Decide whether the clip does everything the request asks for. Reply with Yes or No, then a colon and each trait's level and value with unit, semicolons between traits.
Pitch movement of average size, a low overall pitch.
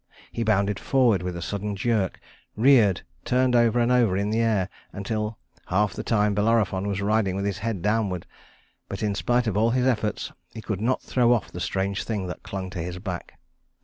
Yes: average, 3.0 semitones; low, 105 Hz